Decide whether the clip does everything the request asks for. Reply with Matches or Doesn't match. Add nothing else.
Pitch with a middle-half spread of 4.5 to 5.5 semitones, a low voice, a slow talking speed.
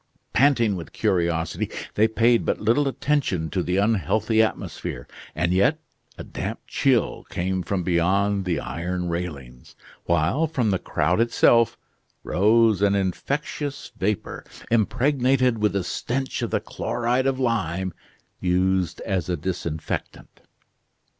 Matches